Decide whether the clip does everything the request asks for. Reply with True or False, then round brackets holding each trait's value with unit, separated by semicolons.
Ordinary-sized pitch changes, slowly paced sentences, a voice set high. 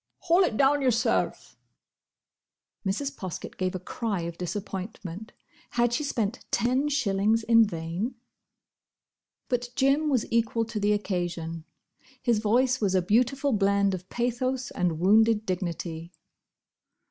True (4.9 semitones; 125 wpm; 215 Hz)